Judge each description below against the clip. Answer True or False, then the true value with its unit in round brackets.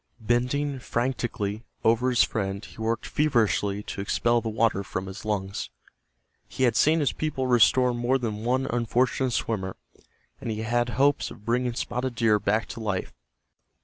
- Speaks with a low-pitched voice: True (115 Hz)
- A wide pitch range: False (3.0 semitones)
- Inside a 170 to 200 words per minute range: False (160 wpm)